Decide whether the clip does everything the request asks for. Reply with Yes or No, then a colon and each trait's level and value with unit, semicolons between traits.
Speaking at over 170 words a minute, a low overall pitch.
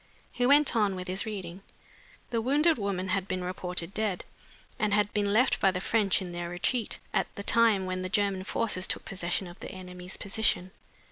No: average, 195 wpm; high, 195 Hz